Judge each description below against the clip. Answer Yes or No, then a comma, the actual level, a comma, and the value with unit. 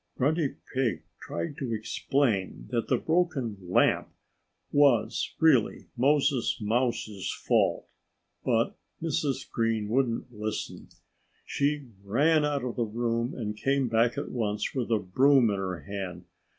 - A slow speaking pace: Yes, slow, 130 wpm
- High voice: No, low, 120 Hz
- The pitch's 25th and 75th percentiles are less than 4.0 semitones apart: No, average, 4.6 semitones